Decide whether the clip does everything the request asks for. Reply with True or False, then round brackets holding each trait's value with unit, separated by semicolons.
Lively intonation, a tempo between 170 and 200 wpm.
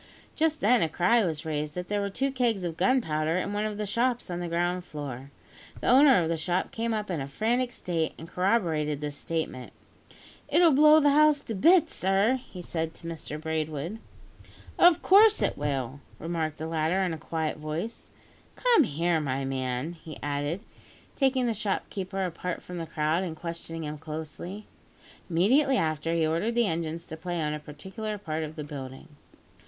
True (5.7 semitones; 185 wpm)